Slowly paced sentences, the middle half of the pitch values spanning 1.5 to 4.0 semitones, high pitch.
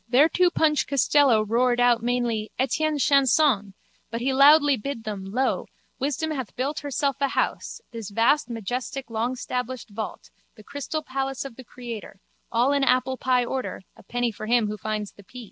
No: average, 165 wpm; average, 3.5 semitones; very high, 250 Hz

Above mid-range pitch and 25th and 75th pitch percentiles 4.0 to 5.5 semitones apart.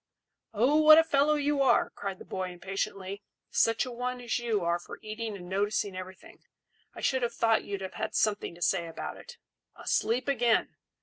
Yes: high, 220 Hz; average, 4.8 semitones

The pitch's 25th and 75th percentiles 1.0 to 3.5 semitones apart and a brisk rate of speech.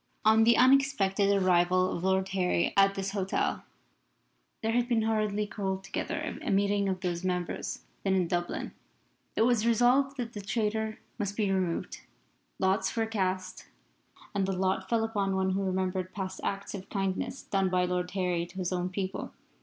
No: narrow, 2.5 semitones; average, 170 wpm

